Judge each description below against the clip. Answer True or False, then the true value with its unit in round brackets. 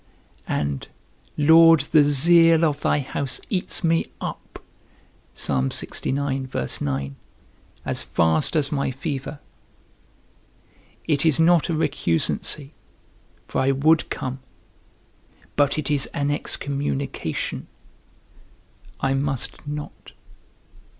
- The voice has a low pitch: False (145 Hz)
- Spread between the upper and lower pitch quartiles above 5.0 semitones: False (2.9 semitones)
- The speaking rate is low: True (90 wpm)